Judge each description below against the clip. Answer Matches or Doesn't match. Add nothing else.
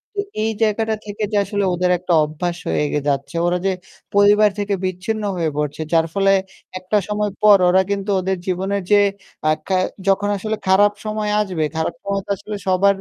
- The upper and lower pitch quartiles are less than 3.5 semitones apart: Matches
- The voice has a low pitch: Doesn't match